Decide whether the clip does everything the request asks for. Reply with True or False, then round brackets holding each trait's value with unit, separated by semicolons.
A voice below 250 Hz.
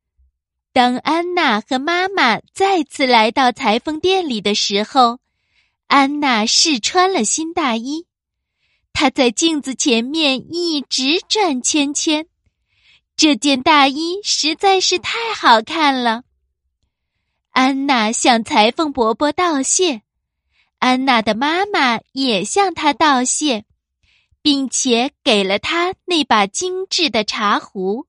False (275 Hz)